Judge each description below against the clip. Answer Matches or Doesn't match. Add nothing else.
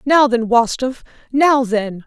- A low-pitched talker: Doesn't match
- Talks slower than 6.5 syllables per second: Matches